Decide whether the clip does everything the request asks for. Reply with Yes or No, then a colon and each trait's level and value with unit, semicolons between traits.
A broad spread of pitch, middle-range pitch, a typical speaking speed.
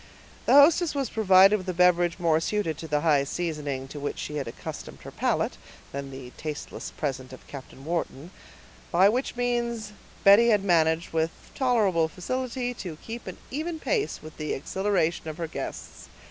Yes: wide, 6.6 semitones; medium, 175 Hz; average, 170 wpm